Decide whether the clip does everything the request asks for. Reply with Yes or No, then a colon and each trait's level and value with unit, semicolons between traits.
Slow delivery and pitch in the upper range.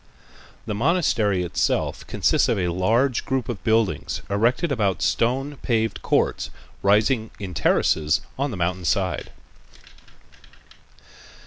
No: slow, 115 wpm; low, 110 Hz